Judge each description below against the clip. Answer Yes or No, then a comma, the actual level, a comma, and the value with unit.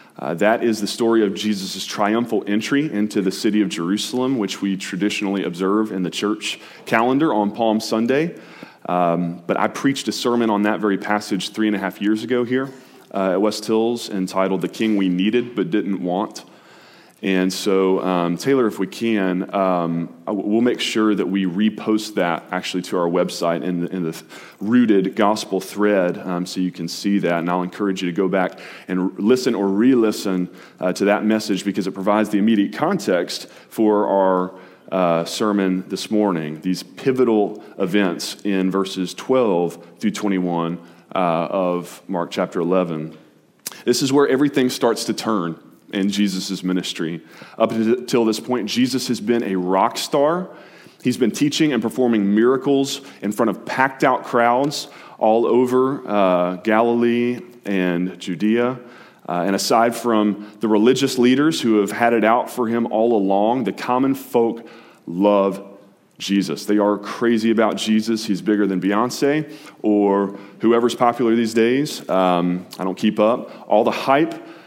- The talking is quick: No, average, 165 wpm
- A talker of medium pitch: No, low, 105 Hz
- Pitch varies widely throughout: No, average, 3.7 semitones